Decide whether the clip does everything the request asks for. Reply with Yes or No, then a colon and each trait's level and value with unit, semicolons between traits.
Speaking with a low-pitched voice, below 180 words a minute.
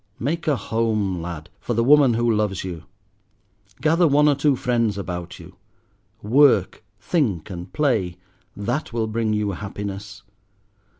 Yes: low, 110 Hz; average, 140 wpm